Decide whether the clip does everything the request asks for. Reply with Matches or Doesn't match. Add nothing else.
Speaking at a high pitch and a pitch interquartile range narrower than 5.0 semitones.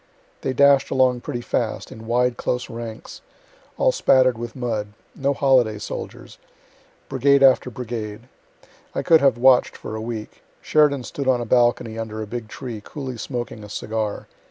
Doesn't match